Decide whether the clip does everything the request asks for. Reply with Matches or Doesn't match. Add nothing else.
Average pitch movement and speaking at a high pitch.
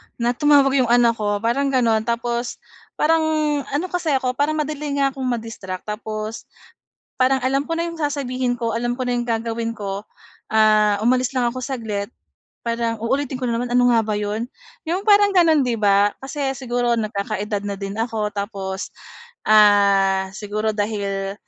Matches